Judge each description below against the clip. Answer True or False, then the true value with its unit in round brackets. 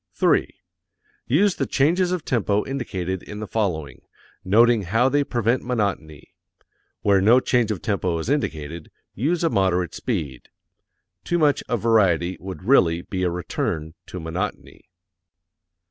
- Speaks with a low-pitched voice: True (105 Hz)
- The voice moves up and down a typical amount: False (5.9 semitones)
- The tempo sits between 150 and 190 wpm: False (140 wpm)